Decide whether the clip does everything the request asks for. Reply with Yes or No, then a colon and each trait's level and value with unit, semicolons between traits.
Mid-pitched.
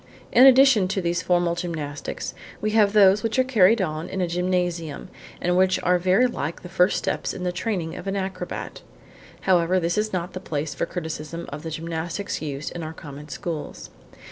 Yes: medium, 180 Hz